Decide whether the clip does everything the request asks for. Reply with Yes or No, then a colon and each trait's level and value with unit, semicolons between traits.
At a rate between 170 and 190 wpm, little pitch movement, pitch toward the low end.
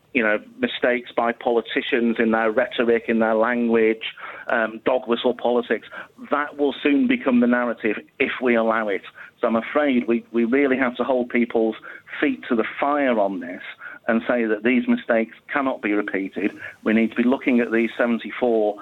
Yes: average, 180 wpm; narrow, 1.5 semitones; low, 120 Hz